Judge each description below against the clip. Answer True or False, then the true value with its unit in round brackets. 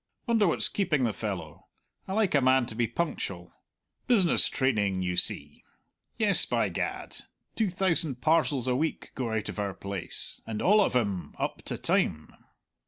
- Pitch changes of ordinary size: False (8.8 semitones)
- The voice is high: False (125 Hz)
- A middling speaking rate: True (170 wpm)